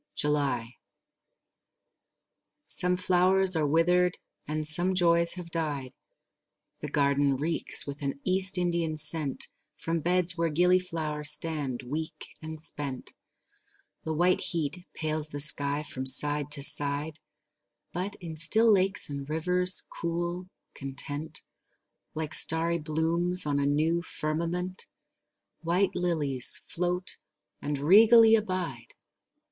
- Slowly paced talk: Yes, slow, 115 wpm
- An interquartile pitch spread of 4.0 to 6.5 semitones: No, average, 3.4 semitones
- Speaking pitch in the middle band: Yes, medium, 160 Hz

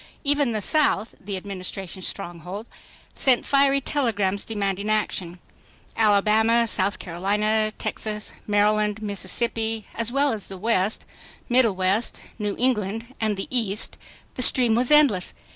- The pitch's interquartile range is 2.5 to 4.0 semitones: Yes, average, 2.9 semitones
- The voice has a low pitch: No, high, 215 Hz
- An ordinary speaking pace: No, slow, 125 wpm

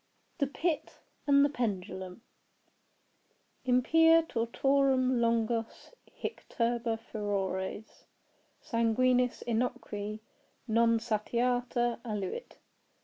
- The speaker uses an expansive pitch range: No, narrow, 2.6 semitones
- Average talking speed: No, slow, 75 wpm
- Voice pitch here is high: Yes, high, 235 Hz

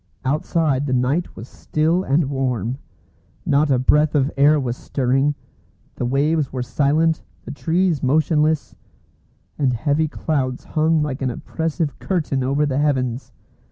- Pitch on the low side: No, medium, 145 Hz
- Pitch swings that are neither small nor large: Yes, average, 3.0 semitones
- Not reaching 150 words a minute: Yes, average, 140 wpm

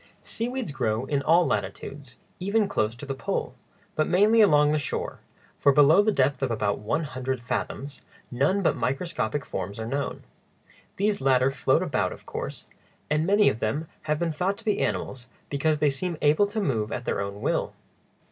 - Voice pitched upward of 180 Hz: No, medium, 145 Hz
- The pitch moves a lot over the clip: Yes, wide, 5.9 semitones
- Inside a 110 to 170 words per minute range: No, average, 185 wpm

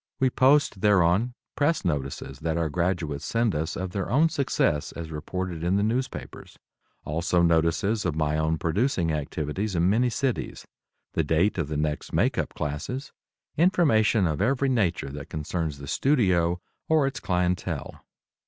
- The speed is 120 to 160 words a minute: Yes, average, 155 wpm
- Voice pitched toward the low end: Yes, very low, 90 Hz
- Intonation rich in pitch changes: Yes, wide, 6.7 semitones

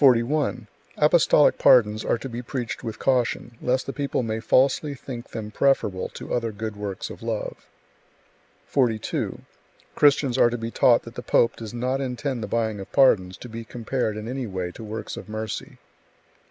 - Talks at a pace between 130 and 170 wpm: No, average, 180 wpm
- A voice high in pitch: No, low, 120 Hz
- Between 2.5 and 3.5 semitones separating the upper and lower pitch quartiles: Yes, average, 3.1 semitones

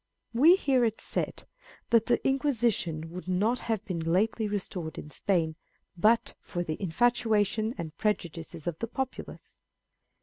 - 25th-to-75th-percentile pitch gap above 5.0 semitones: Yes, wide, 5.5 semitones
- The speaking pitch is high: Yes, high, 210 Hz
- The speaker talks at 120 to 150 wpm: Yes, average, 140 wpm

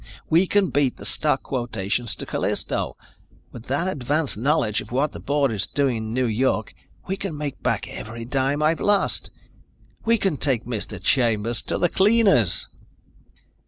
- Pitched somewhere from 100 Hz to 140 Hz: Yes, low, 135 Hz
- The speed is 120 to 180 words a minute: Yes, average, 160 wpm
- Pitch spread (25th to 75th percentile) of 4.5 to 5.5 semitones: Yes, average, 5.2 semitones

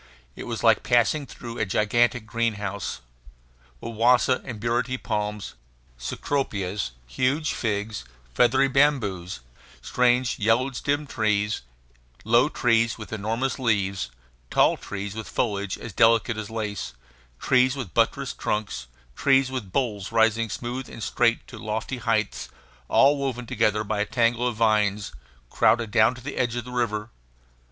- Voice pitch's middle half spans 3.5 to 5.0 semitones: No, average, 2.9 semitones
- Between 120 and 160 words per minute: Yes, average, 140 wpm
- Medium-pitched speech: No, low, 115 Hz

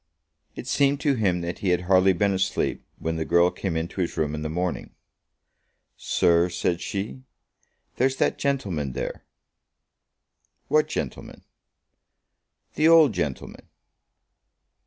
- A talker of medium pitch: No, very low, 90 Hz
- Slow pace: Yes, slow, 130 wpm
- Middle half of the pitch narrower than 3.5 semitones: No, average, 3.8 semitones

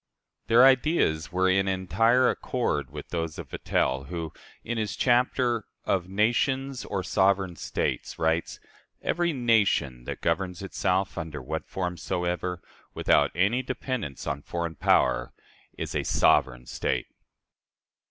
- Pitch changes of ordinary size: No, wide, 6.0 semitones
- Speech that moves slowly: Yes, slow, 130 wpm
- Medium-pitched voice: No, very low, 95 Hz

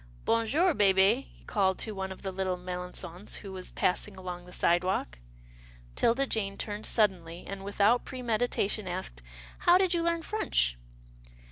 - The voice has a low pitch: No, high, 195 Hz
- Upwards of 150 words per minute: Yes, average, 160 wpm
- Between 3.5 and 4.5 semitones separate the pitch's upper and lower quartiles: Yes, average, 4.0 semitones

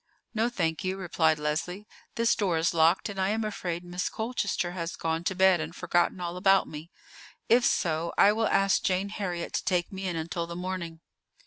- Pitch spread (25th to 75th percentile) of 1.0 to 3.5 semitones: Yes, average, 2.7 semitones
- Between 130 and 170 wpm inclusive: No, average, 200 wpm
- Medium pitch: Yes, medium, 180 Hz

